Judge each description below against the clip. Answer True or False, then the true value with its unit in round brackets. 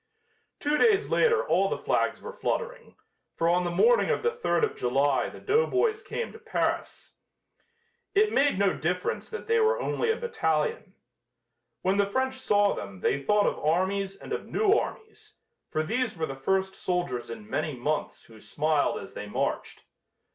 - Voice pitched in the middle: False (200 Hz)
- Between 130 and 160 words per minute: False (175 wpm)